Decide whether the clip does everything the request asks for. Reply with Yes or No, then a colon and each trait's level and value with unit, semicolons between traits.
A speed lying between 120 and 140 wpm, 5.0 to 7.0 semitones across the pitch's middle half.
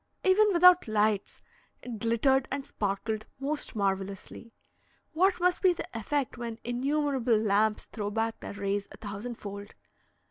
Yes: slow, 135 wpm; wide, 5.4 semitones